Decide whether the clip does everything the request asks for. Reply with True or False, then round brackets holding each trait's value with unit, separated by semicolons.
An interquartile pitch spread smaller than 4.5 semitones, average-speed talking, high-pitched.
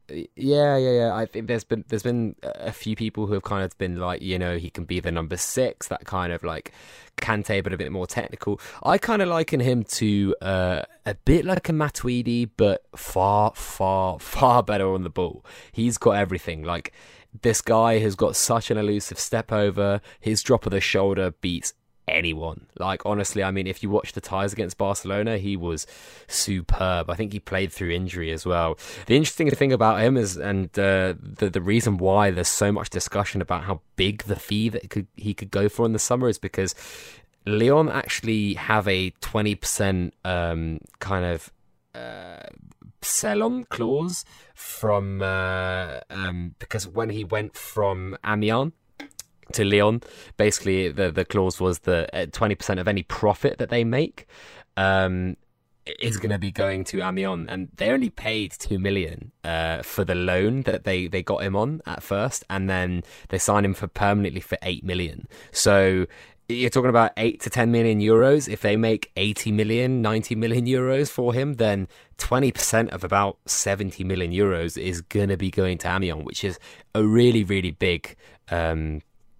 False (3.3 semitones; 185 wpm; 100 Hz)